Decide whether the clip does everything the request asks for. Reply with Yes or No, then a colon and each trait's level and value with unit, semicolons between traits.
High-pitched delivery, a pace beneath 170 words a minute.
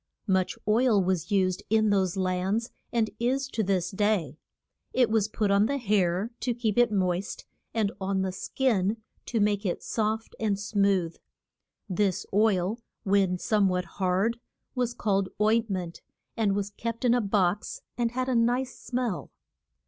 Yes: high, 205 Hz; average, 160 wpm